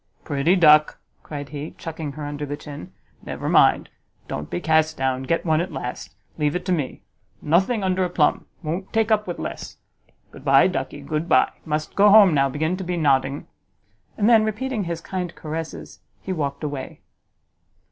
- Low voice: No, medium, 160 Hz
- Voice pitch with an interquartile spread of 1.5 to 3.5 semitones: No, average, 4.0 semitones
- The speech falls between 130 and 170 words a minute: No, average, 180 wpm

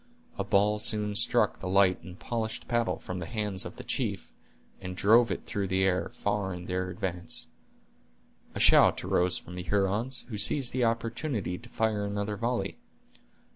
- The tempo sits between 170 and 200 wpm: Yes, average, 175 wpm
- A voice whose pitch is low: Yes, low, 100 Hz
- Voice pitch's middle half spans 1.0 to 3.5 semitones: Yes, average, 3.2 semitones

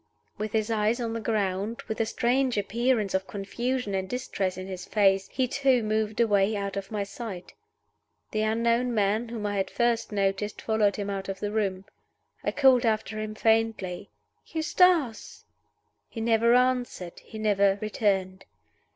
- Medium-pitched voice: No, high, 215 Hz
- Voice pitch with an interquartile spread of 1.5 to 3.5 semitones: Yes, average, 2.9 semitones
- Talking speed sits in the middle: Yes, average, 160 wpm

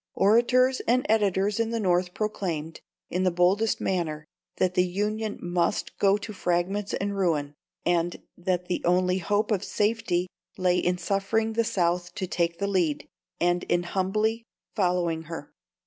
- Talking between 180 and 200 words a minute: No, average, 155 wpm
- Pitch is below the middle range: No, medium, 185 Hz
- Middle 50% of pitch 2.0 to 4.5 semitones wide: Yes, average, 3.0 semitones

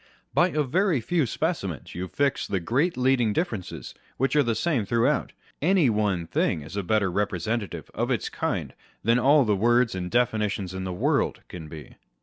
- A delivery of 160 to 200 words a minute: Yes, average, 180 wpm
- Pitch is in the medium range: No, low, 115 Hz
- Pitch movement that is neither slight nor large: No, wide, 6.4 semitones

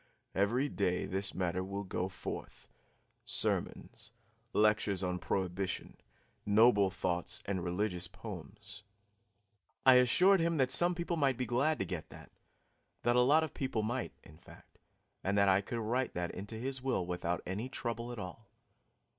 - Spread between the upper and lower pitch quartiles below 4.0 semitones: No, average, 5.2 semitones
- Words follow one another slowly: No, average, 155 wpm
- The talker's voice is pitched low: Yes, low, 105 Hz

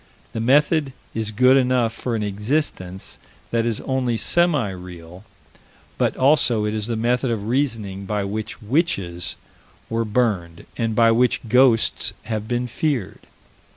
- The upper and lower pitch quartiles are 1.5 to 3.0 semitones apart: No, average, 3.4 semitones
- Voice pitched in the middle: No, low, 115 Hz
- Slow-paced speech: No, average, 145 wpm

